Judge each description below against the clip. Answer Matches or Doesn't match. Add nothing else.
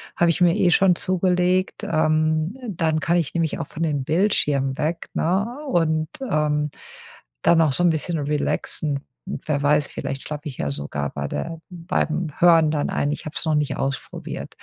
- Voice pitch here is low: Doesn't match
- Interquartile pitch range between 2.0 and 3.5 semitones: Matches